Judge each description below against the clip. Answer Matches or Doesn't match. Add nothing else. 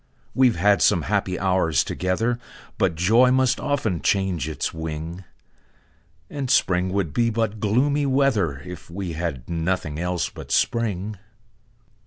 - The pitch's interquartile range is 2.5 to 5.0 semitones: Doesn't match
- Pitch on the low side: Matches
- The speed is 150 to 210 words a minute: Doesn't match